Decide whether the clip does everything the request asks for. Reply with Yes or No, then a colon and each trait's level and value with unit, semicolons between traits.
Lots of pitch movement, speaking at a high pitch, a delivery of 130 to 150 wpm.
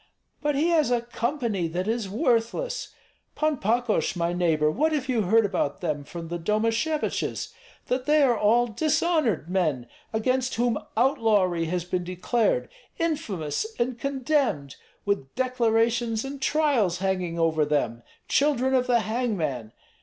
Yes: wide, 6.7 semitones; high, 225 Hz; average, 140 wpm